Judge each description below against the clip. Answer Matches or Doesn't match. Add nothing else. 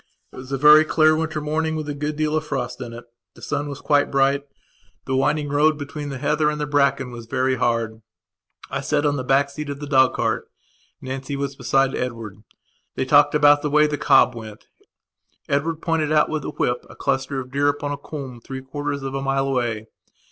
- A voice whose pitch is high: Doesn't match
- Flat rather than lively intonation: Matches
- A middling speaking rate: Doesn't match